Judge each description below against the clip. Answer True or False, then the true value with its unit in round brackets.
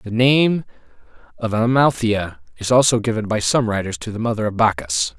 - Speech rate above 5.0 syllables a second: True (5.2 syllables/s)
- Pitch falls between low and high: False (115 Hz)